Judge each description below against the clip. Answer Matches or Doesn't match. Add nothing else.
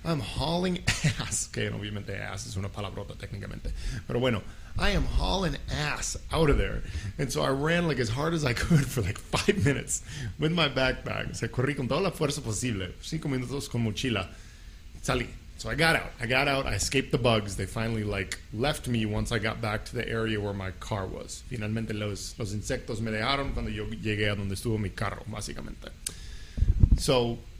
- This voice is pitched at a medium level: Doesn't match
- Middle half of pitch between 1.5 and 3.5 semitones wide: Doesn't match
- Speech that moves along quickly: Doesn't match